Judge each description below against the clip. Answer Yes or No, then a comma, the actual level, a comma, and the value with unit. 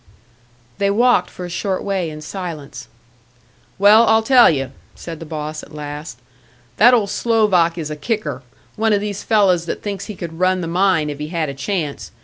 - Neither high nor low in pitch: Yes, medium, 180 Hz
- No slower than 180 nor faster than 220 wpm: Yes, average, 190 wpm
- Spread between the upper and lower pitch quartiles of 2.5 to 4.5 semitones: No, average, 5.0 semitones